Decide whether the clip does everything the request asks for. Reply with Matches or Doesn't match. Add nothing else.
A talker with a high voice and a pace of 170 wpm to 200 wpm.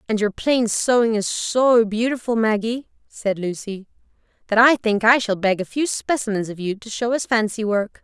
Matches